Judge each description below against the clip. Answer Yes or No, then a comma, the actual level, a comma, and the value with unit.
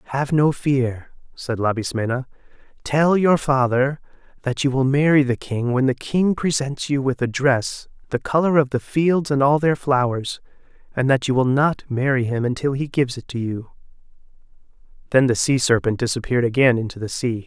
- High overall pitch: No, low, 130 Hz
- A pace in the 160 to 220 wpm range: Yes, average, 180 wpm